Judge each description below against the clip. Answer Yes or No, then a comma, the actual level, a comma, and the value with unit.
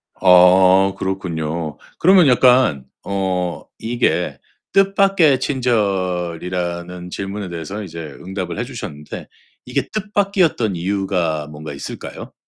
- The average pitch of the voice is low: Yes, very low, 95 Hz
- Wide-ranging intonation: Yes, wide, 5.8 semitones